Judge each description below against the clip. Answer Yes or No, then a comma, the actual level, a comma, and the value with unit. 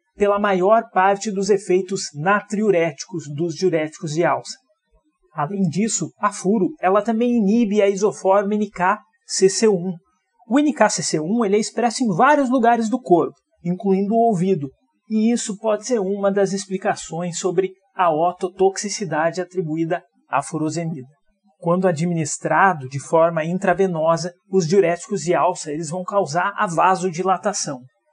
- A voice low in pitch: No, high, 190 Hz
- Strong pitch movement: No, average, 3.3 semitones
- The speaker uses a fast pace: No, average, 130 wpm